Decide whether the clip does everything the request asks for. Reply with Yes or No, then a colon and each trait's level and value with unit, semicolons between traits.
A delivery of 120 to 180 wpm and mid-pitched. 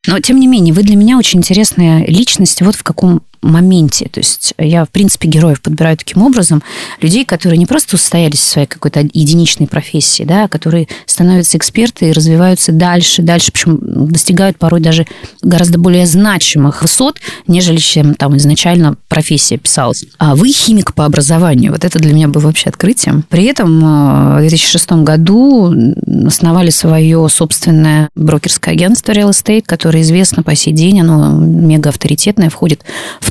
Yes: fast, 160 wpm; medium, 165 Hz